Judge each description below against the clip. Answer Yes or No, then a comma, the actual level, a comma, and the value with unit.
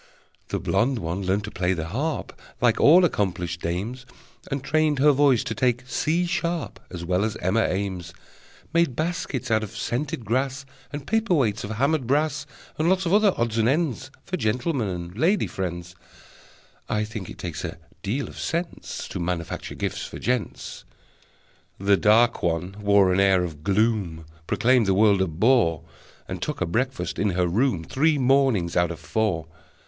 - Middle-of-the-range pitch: No, low, 110 Hz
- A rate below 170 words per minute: No, average, 175 wpm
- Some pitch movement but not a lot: No, wide, 6.9 semitones